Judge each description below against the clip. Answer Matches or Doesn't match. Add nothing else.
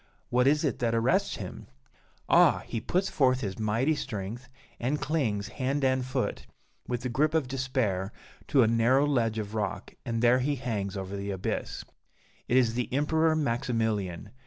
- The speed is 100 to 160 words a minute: Doesn't match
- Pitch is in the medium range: Doesn't match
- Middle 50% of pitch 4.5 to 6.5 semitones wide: Doesn't match